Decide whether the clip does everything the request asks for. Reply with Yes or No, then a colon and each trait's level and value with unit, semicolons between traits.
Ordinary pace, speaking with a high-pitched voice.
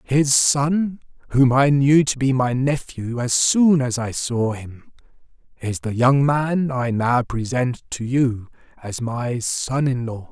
No: average, 170 wpm; low, 130 Hz